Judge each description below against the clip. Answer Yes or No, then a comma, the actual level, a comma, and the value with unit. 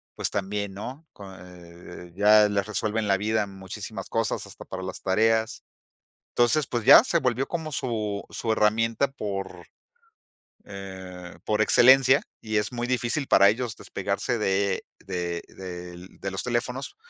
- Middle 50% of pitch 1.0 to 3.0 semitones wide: No, average, 3.6 semitones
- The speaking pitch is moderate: No, low, 105 Hz